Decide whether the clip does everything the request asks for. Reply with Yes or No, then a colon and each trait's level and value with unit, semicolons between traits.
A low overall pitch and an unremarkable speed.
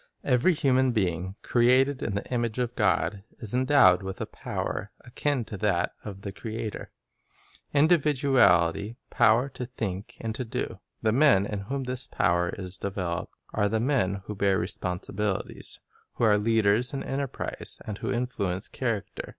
Yes: low, 110 Hz; average, 160 wpm